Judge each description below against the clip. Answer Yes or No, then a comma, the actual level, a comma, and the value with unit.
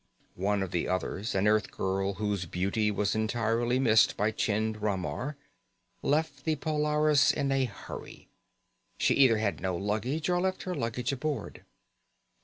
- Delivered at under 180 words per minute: Yes, average, 145 wpm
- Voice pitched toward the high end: No, low, 110 Hz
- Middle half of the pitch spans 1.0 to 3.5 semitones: No, wide, 5.6 semitones